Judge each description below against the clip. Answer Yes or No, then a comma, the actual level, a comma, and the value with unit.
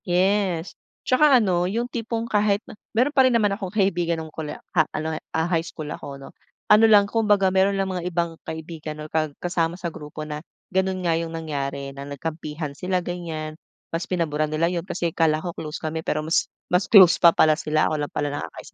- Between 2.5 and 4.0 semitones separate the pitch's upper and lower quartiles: Yes, average, 3.6 semitones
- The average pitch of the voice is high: No, medium, 170 Hz